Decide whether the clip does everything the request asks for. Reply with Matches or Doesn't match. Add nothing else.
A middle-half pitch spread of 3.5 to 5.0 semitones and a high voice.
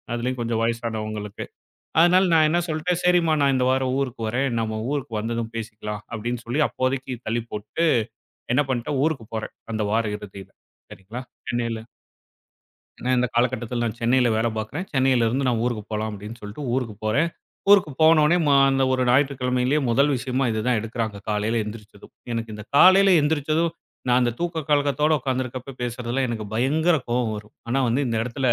Doesn't match